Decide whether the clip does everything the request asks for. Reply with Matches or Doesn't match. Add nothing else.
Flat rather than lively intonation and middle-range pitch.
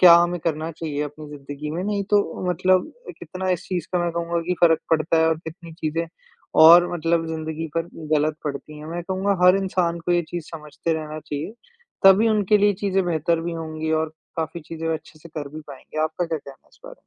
Matches